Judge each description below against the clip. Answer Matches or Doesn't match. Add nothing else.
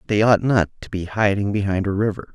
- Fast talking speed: Matches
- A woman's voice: Doesn't match